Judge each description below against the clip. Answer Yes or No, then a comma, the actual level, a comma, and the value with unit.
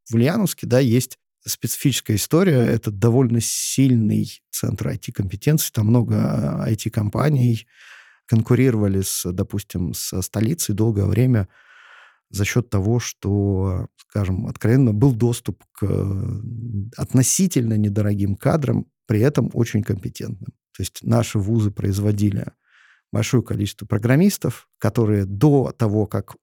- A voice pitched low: Yes, low, 115 Hz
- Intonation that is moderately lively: Yes, average, 3.3 semitones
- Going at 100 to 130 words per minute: Yes, average, 115 wpm